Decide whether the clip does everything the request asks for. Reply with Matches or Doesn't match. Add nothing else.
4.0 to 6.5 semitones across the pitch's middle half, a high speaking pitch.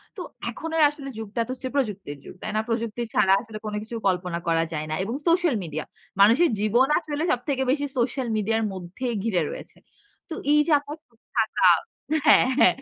Matches